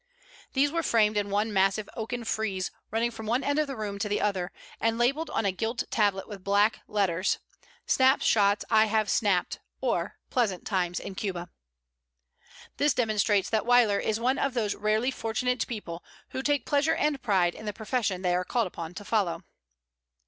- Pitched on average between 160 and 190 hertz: No, high, 215 Hz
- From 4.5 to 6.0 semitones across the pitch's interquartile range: No, average, 3.4 semitones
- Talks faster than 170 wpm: Yes, average, 185 wpm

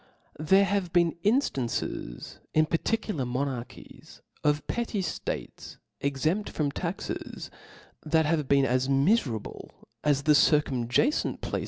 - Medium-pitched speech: Yes, medium, 150 Hz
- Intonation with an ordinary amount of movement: Yes, average, 4.7 semitones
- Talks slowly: Yes, slow, 120 wpm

